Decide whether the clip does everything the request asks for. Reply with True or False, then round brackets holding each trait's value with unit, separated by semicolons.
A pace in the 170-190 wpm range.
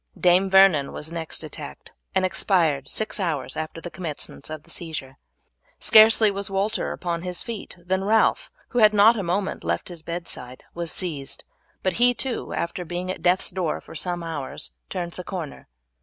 True (180 wpm)